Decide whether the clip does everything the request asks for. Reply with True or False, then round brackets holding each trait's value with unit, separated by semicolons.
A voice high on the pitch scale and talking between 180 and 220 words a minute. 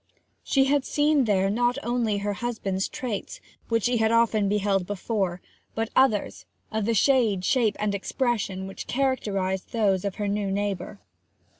False (210 Hz; 155 wpm)